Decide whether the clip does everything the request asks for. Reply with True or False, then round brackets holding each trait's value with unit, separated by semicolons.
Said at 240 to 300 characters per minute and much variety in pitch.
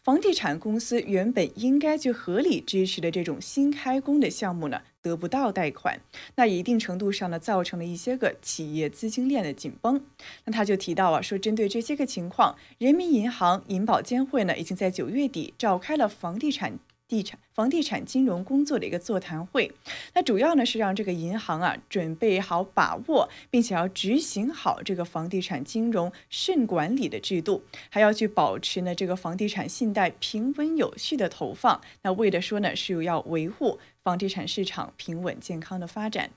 True (290 characters per minute; 5.8 semitones)